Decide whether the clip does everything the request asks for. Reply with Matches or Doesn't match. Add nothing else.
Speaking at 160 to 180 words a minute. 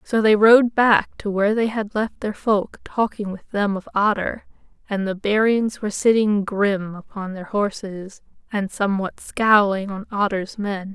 Matches